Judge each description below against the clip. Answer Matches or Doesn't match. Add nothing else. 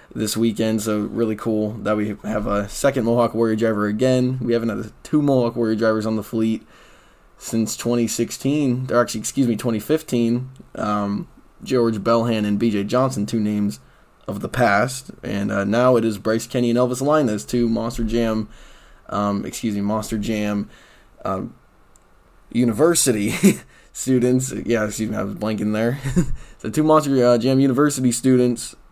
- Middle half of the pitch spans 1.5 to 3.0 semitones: Matches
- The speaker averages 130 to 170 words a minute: Matches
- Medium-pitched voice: Doesn't match